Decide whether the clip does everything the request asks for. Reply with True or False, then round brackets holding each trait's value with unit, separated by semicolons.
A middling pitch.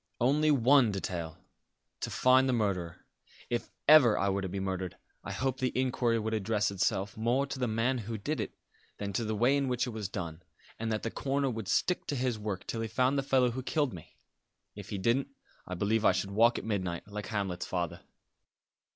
False (110 Hz)